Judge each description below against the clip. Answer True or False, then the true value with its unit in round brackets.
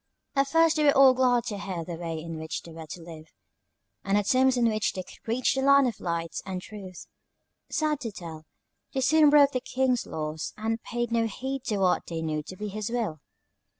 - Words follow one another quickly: True (220 wpm)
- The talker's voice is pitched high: True (220 Hz)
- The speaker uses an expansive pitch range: True (7.4 semitones)